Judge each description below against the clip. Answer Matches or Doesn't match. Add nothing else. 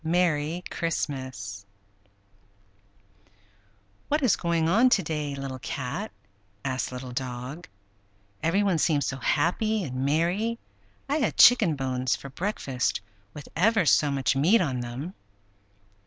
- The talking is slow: Matches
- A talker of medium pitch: Matches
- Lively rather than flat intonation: Matches